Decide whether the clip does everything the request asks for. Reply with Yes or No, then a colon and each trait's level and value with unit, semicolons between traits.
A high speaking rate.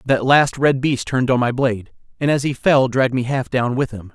Yes: fast, 260 wpm